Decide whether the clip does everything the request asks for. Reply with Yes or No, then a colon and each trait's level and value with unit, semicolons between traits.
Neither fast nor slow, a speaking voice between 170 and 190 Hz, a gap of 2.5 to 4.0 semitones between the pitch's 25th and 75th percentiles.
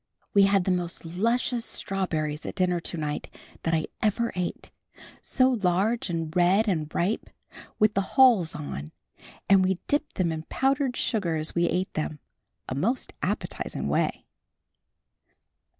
No: average, 150 wpm; medium, 185 Hz; average, 4.9 semitones